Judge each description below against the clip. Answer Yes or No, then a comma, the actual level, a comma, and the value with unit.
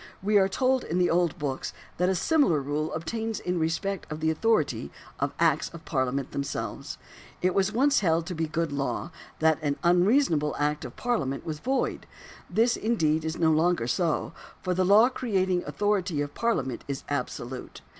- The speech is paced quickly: No, average, 175 wpm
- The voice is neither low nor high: Yes, medium, 165 Hz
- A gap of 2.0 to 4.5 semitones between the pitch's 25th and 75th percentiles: No, average, 4.9 semitones